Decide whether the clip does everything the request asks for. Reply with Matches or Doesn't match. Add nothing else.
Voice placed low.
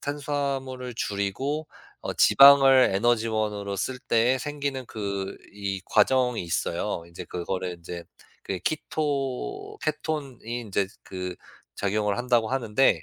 Matches